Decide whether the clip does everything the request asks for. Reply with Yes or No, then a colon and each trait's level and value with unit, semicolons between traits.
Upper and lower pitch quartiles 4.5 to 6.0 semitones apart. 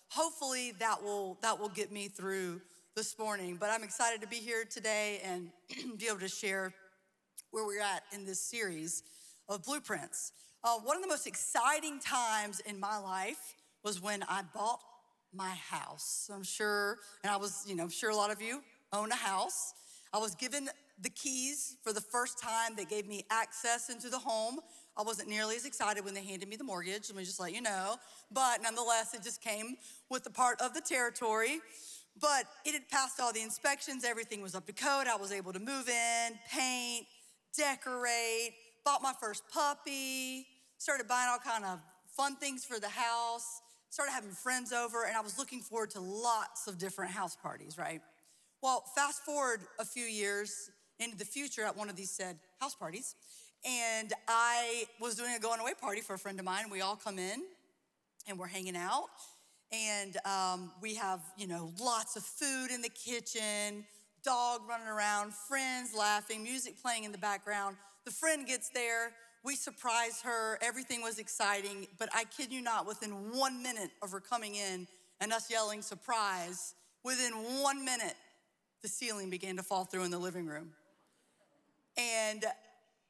No: average, 3.7 semitones